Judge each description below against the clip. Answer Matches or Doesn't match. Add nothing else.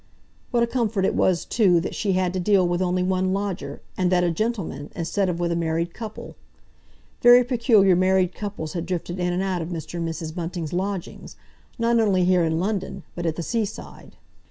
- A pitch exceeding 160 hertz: Matches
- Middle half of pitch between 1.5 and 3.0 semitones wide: Matches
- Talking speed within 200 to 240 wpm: Matches